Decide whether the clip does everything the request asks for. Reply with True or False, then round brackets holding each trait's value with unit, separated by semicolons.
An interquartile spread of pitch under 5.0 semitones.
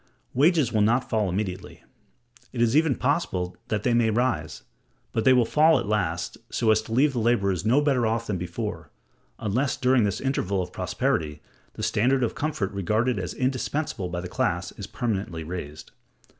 False (5.3 semitones)